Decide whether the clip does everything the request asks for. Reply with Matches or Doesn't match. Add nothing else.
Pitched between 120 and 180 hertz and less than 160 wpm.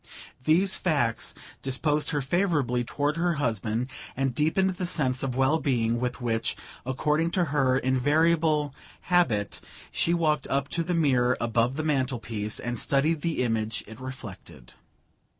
Matches